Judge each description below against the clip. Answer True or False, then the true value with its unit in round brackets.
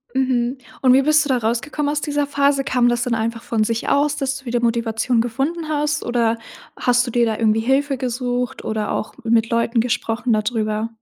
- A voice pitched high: True (245 Hz)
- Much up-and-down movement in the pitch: False (3.1 semitones)